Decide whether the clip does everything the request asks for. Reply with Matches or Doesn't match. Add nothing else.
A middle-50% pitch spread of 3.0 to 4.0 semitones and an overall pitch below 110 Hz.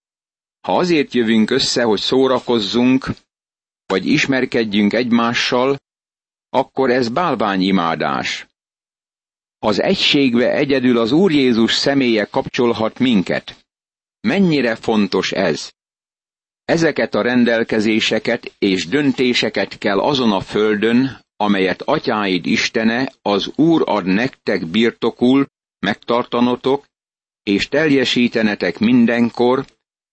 Doesn't match